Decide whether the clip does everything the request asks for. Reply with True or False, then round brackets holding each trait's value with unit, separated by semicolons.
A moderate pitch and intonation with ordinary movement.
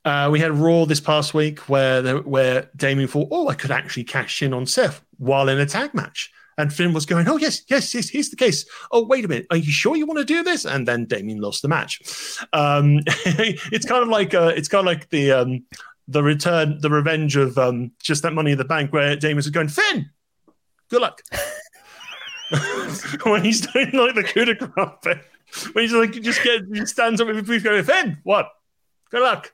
False (160 Hz; 7.8 semitones)